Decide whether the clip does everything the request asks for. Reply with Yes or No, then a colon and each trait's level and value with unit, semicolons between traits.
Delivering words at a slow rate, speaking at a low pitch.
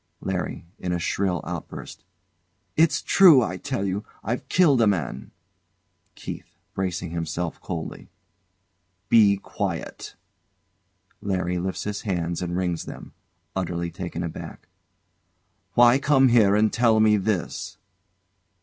Yes: slow, 120 wpm; very low, 95 Hz